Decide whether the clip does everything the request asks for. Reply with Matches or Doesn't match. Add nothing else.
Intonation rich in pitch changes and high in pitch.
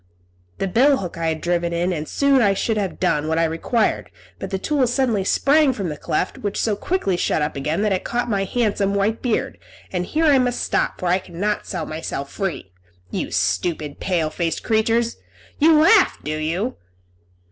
Matches